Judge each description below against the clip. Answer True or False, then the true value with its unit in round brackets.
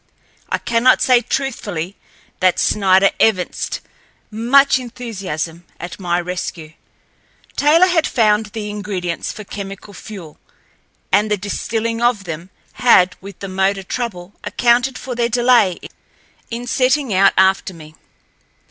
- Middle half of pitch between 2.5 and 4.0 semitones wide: False (4.5 semitones)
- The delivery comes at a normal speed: False (125 wpm)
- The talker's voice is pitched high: True (205 Hz)